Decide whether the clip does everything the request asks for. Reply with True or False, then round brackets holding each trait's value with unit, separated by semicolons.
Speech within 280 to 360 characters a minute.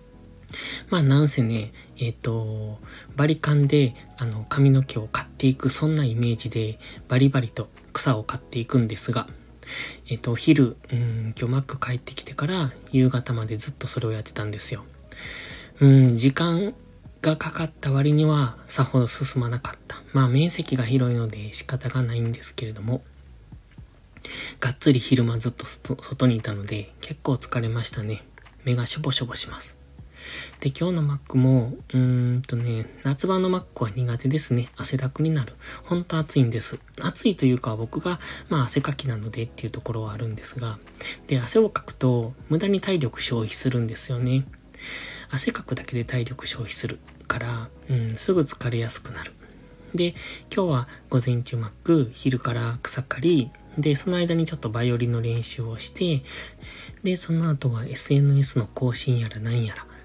True (330 characters per minute)